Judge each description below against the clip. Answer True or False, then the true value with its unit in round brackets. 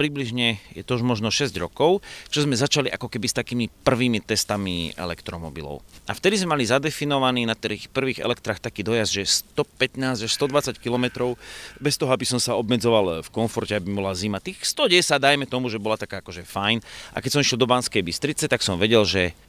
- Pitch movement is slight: False (4.2 semitones)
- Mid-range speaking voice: False (120 Hz)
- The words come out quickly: True (190 wpm)